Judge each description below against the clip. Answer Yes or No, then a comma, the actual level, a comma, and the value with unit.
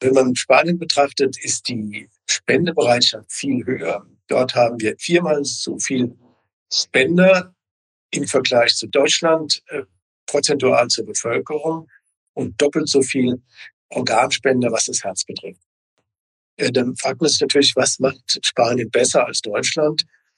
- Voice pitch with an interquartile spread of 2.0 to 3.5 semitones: No, average, 4.2 semitones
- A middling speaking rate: Yes, average, 135 wpm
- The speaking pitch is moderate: No, low, 130 Hz